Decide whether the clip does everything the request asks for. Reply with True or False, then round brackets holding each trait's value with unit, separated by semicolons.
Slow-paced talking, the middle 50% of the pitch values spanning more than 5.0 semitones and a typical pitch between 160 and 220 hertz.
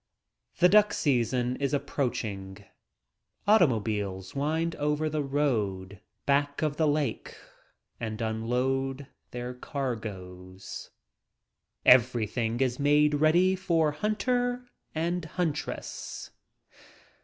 False (95 wpm; 5.4 semitones; 140 Hz)